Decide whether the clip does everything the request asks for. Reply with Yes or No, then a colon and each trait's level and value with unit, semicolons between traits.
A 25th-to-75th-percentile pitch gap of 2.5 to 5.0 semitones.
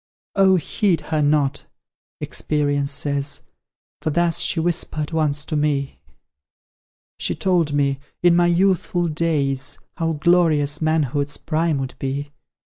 Yes: average, 2.9 semitones